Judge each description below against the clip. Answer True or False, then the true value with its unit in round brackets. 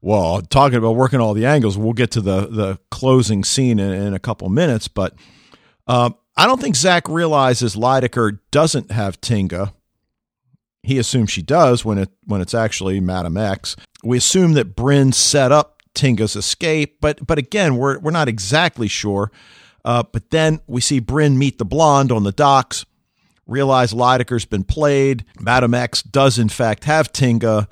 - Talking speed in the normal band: True (175 wpm)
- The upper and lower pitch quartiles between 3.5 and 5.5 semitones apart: True (4.7 semitones)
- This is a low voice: True (120 Hz)